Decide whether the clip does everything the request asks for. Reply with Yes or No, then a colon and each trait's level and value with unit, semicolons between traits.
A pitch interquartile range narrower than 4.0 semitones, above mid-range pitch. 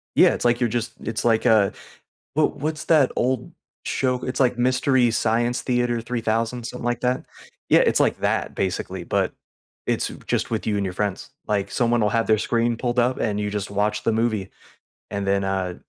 No: average, 2.9 semitones; low, 115 Hz